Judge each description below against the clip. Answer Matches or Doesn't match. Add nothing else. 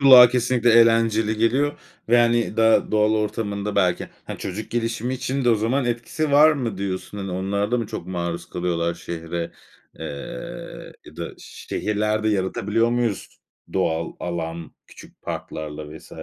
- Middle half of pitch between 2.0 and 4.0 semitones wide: Doesn't match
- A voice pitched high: Doesn't match